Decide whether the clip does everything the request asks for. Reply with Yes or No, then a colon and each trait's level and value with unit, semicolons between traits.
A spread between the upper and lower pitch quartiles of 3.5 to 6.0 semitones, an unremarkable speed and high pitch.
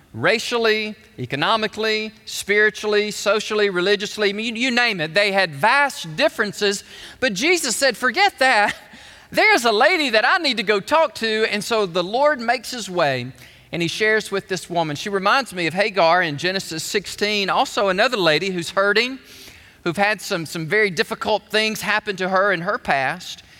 No: average, 2.8 semitones; average, 170 wpm; high, 210 Hz